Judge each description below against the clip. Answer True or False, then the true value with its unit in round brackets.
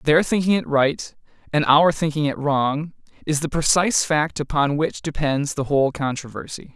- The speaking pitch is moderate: True (150 Hz)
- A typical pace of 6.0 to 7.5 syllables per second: False (4.8 syllables/s)